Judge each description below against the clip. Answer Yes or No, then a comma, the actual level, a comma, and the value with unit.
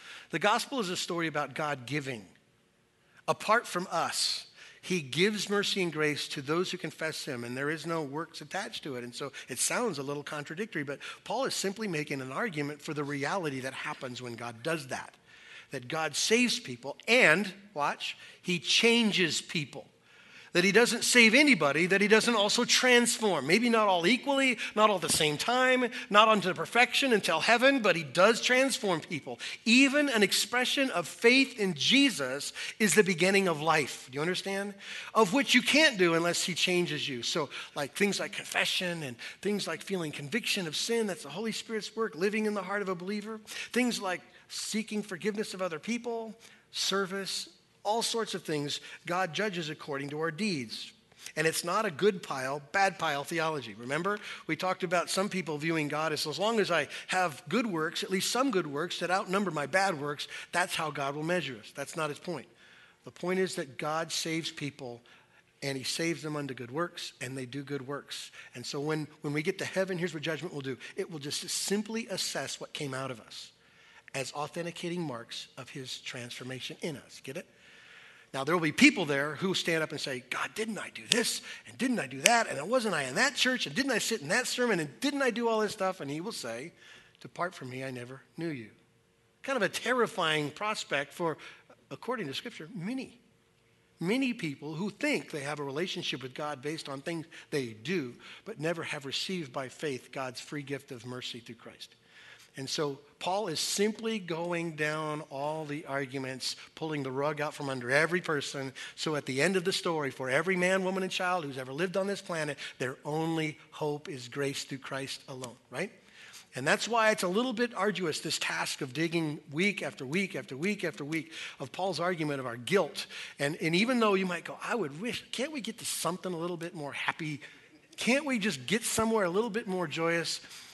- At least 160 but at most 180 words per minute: No, fast, 205 wpm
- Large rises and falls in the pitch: Yes, wide, 5.9 semitones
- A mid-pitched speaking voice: Yes, medium, 170 Hz